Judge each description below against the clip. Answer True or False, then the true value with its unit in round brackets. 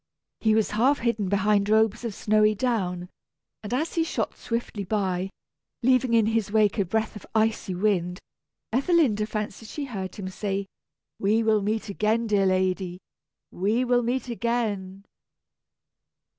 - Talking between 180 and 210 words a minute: False (145 wpm)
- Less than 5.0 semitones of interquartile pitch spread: True (2.9 semitones)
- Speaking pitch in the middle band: False (215 Hz)